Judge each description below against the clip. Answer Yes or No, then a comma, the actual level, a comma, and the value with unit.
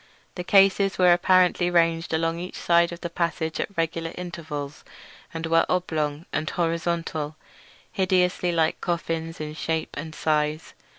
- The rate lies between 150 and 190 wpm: No, average, 140 wpm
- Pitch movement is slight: Yes, narrow, 1.8 semitones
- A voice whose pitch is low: No, medium, 165 Hz